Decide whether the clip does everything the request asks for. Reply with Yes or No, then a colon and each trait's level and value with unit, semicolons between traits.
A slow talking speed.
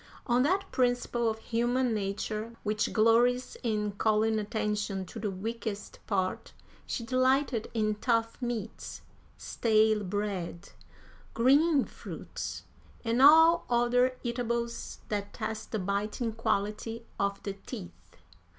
Yes: slow, 115 wpm